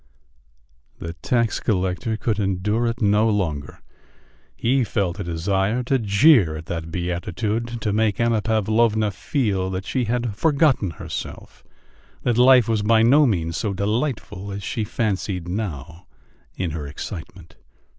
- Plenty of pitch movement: No, average, 4.2 semitones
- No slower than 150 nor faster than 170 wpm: No, average, 140 wpm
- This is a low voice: Yes, low, 105 Hz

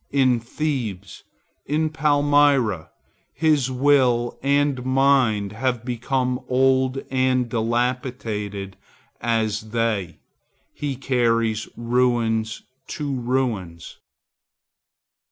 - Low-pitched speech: Yes, low, 125 Hz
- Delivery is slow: Yes, slow, 80 wpm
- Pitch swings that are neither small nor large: Yes, average, 3.1 semitones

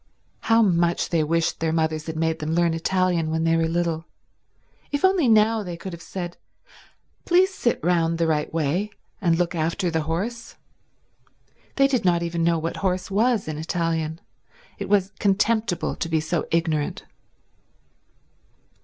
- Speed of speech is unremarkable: Yes, average, 160 wpm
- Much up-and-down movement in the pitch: No, average, 3.3 semitones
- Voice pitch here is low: No, medium, 170 Hz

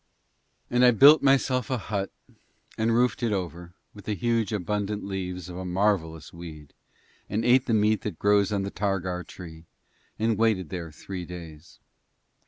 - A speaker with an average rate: Yes, average, 165 wpm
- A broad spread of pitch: No, average, 4.0 semitones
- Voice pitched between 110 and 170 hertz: No, low, 100 Hz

